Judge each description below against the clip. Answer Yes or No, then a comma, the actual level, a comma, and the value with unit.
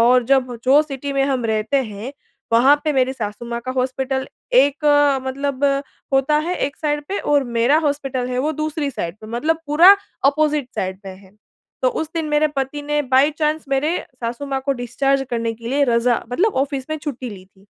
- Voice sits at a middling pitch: No, very high, 270 Hz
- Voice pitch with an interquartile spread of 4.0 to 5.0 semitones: No, average, 3.3 semitones